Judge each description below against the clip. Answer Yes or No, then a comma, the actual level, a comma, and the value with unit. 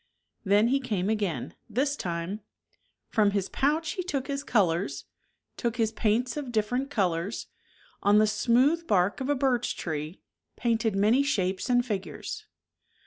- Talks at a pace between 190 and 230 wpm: No, average, 145 wpm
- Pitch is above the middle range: Yes, high, 225 Hz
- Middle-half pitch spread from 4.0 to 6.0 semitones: Yes, average, 5.2 semitones